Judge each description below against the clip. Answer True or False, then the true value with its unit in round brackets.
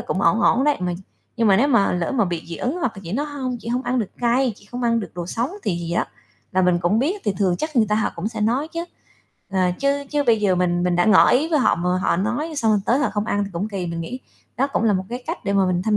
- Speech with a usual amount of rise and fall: False (5.8 semitones)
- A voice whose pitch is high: True (220 Hz)